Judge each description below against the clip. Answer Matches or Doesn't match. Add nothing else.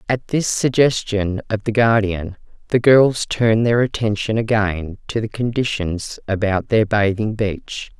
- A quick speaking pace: Doesn't match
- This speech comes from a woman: Matches